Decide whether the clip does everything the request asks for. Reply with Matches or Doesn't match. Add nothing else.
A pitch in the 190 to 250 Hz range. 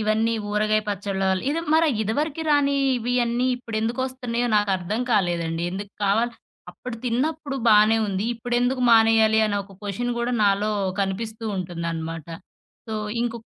Matches